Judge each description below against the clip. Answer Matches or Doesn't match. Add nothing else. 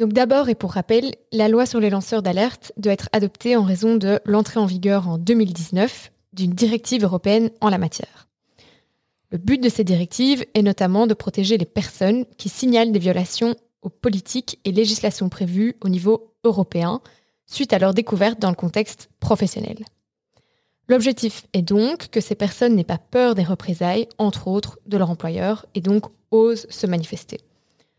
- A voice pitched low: Doesn't match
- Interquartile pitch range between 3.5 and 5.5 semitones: Doesn't match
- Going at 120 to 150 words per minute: Doesn't match